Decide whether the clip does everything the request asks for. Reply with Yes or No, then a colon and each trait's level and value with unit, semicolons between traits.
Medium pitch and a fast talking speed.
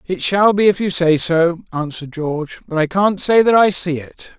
Yes: medium, 175 Hz; fast, 235 wpm